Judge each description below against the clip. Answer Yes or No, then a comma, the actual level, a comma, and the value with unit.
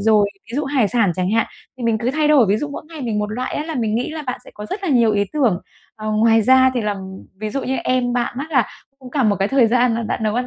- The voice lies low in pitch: No, high, 240 Hz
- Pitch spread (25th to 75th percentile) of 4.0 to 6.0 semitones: No, average, 3.6 semitones